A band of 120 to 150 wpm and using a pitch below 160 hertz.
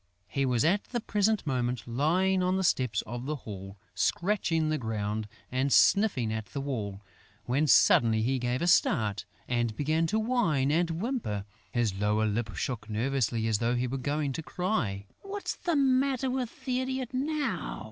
No: average, 175 wpm; medium, 140 Hz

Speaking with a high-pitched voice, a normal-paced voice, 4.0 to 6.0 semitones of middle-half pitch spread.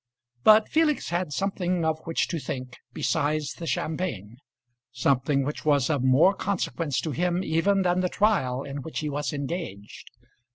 No: medium, 155 Hz; average, 160 wpm; average, 4.7 semitones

